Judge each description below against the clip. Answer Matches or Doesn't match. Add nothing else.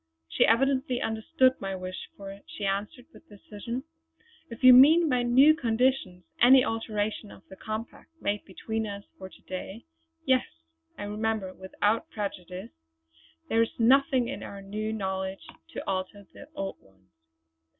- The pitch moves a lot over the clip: Doesn't match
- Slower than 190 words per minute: Matches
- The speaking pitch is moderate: Doesn't match